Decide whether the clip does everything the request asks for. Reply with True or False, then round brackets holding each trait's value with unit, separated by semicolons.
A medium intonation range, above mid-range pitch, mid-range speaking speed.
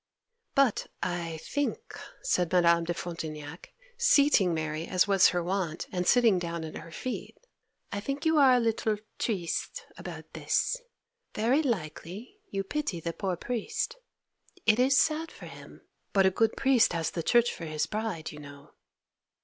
False (6.8 semitones; 195 Hz; 160 wpm)